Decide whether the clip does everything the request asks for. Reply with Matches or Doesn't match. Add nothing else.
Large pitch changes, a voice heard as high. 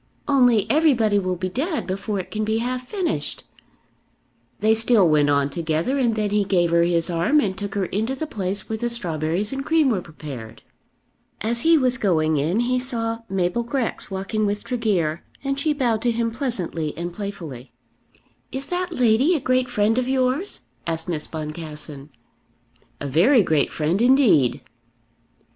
Matches